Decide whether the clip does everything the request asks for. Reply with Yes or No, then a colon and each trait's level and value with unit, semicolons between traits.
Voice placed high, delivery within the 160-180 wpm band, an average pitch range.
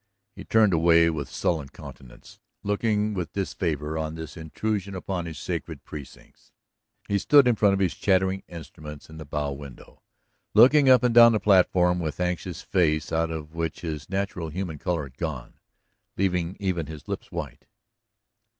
No: very low, 85 Hz; average, 165 wpm; average, 4.0 semitones